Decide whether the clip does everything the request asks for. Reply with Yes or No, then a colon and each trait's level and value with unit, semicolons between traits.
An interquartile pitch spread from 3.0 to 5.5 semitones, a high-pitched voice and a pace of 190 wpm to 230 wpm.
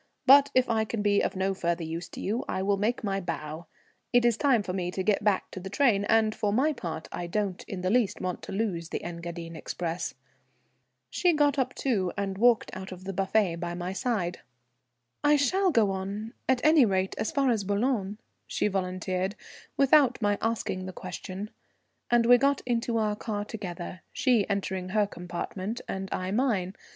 Yes: average, 4.1 semitones; high, 200 Hz; average, 195 wpm